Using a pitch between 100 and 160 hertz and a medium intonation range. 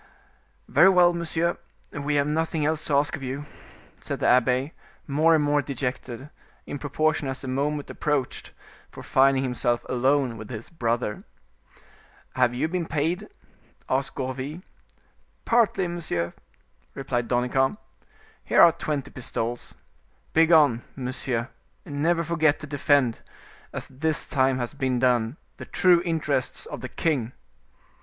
Yes: medium, 140 Hz; average, 3.8 semitones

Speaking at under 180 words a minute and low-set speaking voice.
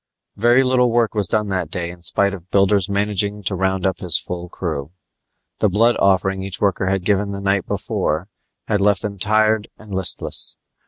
No: average, 190 wpm; low, 100 Hz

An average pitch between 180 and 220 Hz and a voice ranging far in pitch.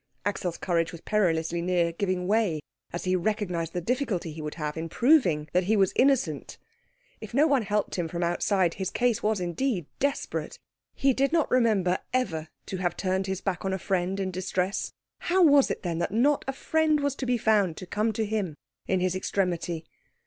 No: high, 190 Hz; average, 4.6 semitones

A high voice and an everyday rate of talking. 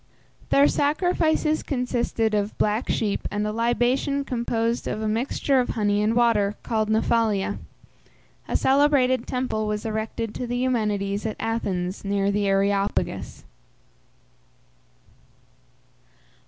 No: high, 225 Hz; slow, 115 wpm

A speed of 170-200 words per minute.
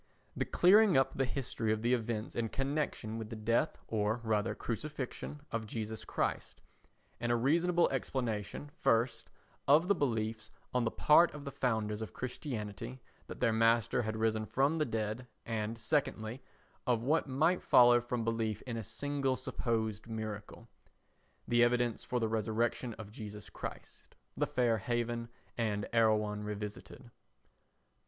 No: average, 150 wpm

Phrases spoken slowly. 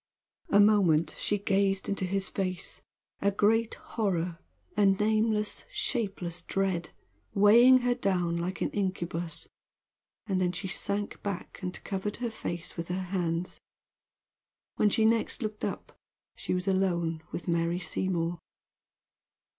Yes: slow, 130 wpm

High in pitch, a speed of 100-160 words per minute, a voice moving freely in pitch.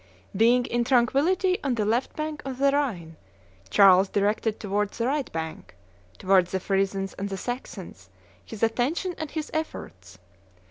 Yes: high, 225 Hz; average, 150 wpm; wide, 6.1 semitones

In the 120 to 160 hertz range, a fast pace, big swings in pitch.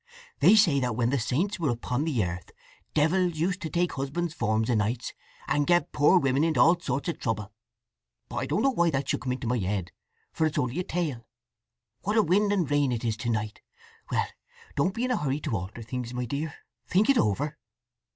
Yes: medium, 140 Hz; fast, 220 wpm; wide, 6.5 semitones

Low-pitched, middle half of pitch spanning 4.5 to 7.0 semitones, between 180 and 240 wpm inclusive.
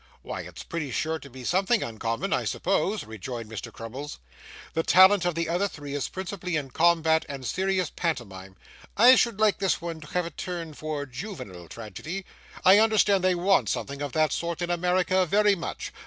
No: medium, 170 Hz; average, 5.2 semitones; average, 185 wpm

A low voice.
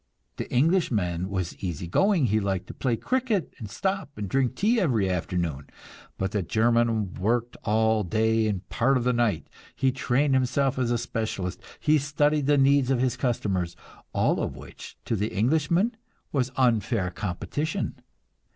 Yes: low, 120 Hz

